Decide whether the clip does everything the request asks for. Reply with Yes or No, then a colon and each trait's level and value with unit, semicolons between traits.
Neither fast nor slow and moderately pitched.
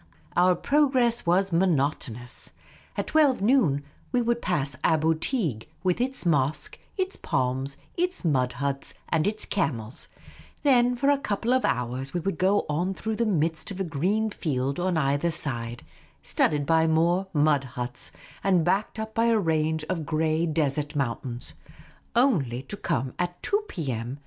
Yes: average, 160 wpm; medium, 165 Hz